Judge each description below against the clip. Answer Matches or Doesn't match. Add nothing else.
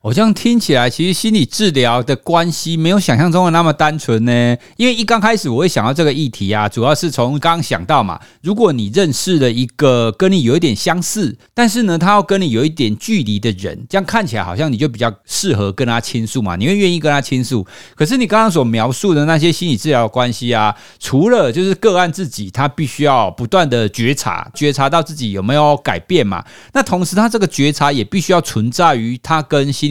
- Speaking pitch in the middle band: Matches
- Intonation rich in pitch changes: Matches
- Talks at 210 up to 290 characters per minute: Doesn't match